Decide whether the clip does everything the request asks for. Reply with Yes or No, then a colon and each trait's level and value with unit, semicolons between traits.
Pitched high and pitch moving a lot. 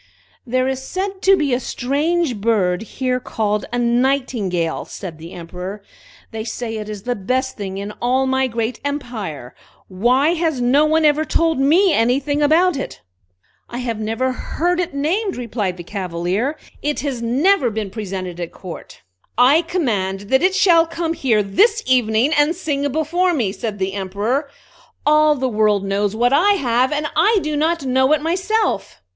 Yes: very high, 255 Hz; wide, 6.4 semitones